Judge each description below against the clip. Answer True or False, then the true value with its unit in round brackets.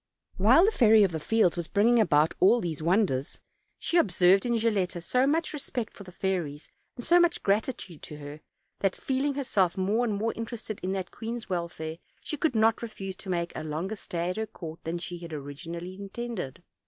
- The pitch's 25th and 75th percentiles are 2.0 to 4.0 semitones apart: False (5.1 semitones)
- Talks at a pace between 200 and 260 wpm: True (205 wpm)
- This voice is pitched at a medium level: False (195 Hz)